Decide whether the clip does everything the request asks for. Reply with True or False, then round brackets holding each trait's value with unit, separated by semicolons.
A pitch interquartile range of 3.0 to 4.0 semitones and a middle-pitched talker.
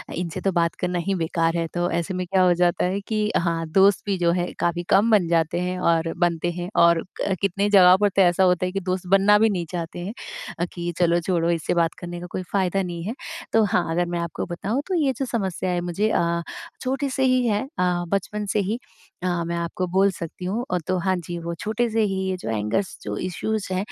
False (2.5 semitones; 180 Hz)